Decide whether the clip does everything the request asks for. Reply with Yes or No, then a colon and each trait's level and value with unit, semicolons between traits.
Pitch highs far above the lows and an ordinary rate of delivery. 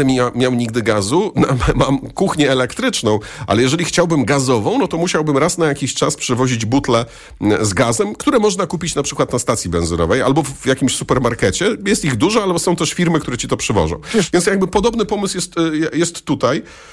No: wide, 5.8 semitones; fast, 180 wpm